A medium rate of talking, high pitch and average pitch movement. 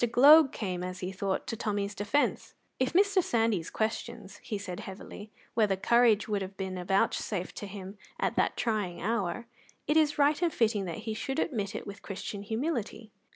Yes: average, 180 wpm; high, 210 Hz; average, 3.6 semitones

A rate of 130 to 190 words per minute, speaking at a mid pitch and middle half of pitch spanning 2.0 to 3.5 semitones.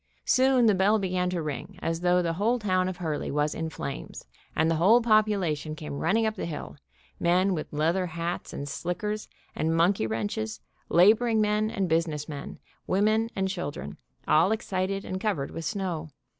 No: average, 180 wpm; medium, 180 Hz; average, 4.8 semitones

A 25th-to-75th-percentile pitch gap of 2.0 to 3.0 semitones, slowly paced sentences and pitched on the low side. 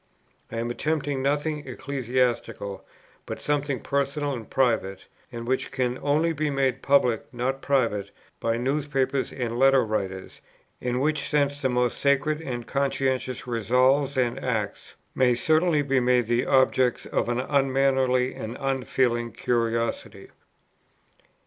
Yes: average, 2.7 semitones; slow, 130 wpm; low, 130 Hz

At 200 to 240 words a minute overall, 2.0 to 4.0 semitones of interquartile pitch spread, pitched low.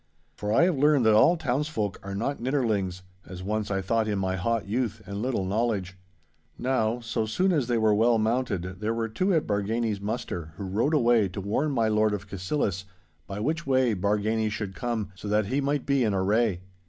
Yes: fast, 205 wpm; average, 3.6 semitones; low, 110 Hz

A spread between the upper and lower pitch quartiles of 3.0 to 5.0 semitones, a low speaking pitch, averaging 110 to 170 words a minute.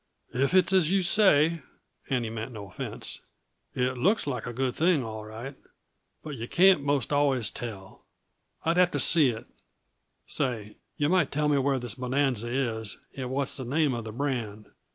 No: average, 4.2 semitones; low, 130 Hz; average, 180 wpm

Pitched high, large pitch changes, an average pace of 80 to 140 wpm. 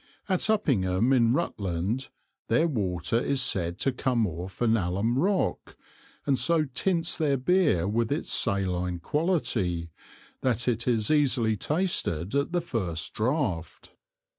No: low, 120 Hz; wide, 7.9 semitones; slow, 135 wpm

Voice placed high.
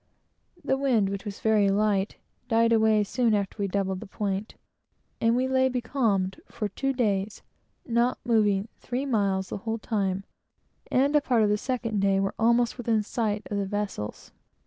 Yes: high, 215 Hz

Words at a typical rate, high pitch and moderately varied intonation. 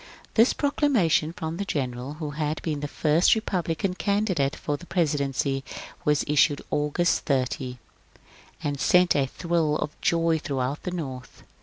No: average, 150 wpm; medium, 150 Hz; average, 3.7 semitones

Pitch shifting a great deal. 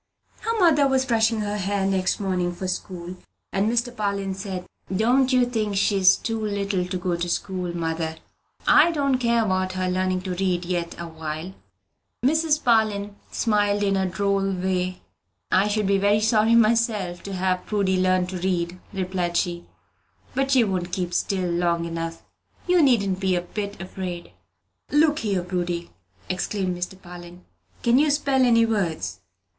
No: average, 3.6 semitones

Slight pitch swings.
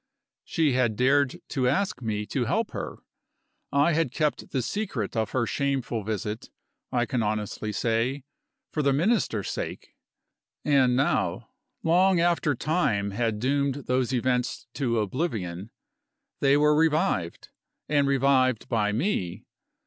No: average, 4.6 semitones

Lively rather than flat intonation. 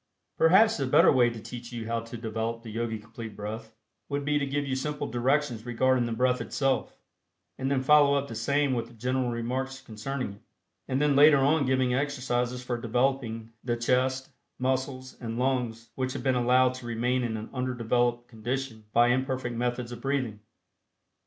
No: narrow, 2.4 semitones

